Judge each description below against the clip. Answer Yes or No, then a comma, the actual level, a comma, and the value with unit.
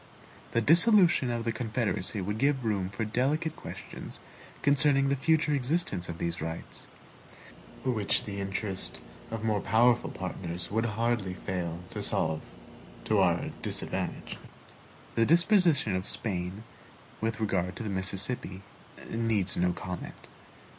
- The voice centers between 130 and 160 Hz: No, low, 110 Hz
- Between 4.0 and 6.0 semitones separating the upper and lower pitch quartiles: Yes, wide, 5.5 semitones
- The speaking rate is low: Yes, slow, 130 wpm